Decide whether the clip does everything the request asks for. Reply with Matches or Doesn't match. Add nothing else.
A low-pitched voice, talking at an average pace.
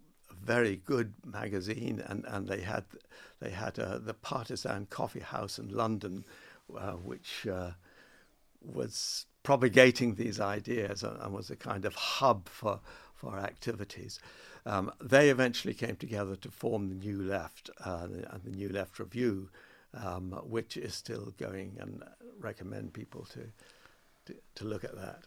Matches